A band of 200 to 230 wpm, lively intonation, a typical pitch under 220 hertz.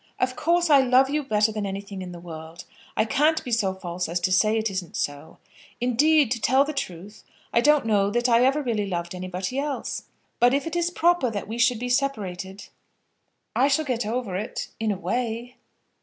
No: fast, 205 wpm; wide, 6.0 semitones; high, 225 Hz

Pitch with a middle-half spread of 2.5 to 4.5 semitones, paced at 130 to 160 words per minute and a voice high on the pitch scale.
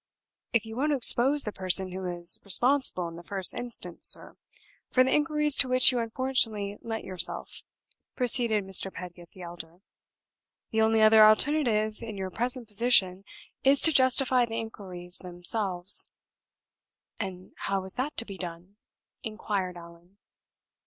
No: average, 5.0 semitones; average, 145 wpm; high, 215 Hz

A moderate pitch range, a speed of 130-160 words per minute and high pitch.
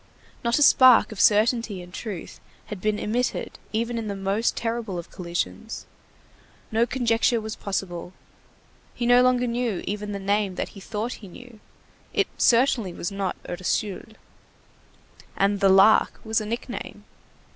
Yes: average, 3.2 semitones; average, 150 wpm; high, 215 Hz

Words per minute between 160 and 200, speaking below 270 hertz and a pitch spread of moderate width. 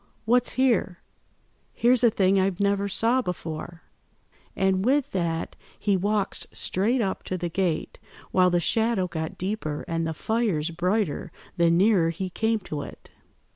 No: average, 150 wpm; high, 190 Hz; average, 4.3 semitones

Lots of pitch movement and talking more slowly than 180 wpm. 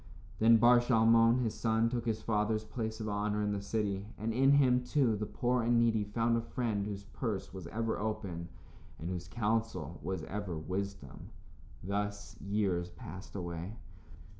No: average, 2.7 semitones; average, 165 wpm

